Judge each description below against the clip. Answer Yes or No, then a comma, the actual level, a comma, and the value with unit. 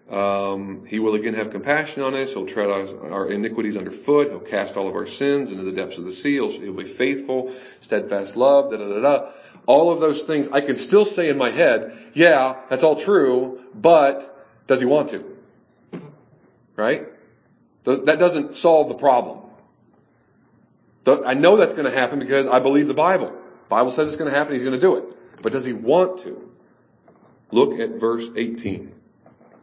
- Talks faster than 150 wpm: Yes, average, 180 wpm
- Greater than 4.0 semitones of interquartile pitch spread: Yes, average, 4.9 semitones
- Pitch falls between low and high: No, low, 130 Hz